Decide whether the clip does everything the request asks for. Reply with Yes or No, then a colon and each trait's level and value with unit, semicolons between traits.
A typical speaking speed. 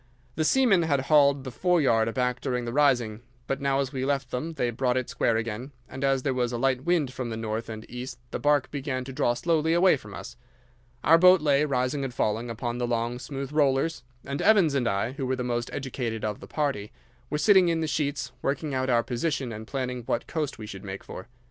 No: fast, 230 wpm